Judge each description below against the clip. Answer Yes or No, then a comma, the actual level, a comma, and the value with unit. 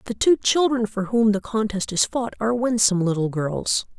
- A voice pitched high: Yes, high, 215 Hz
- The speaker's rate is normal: Yes, average, 195 wpm